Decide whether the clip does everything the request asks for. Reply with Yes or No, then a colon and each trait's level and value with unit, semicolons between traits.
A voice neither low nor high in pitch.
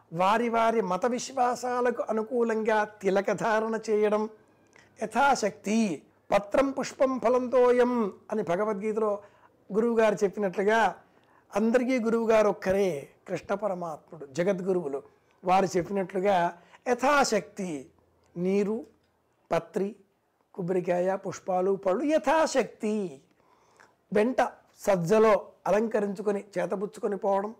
No: high, 210 Hz